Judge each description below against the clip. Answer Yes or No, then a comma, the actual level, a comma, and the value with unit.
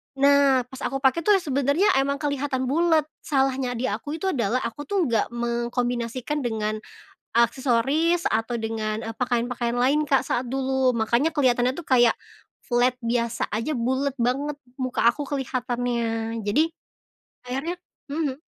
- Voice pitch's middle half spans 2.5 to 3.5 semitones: Yes, average, 3.1 semitones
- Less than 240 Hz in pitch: No, very high, 255 Hz